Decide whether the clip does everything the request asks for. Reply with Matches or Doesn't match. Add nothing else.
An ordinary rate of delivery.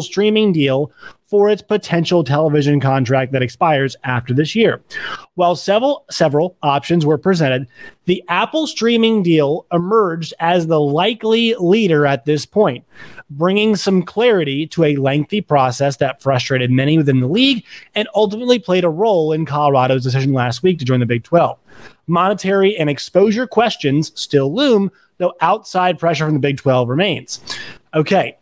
Matches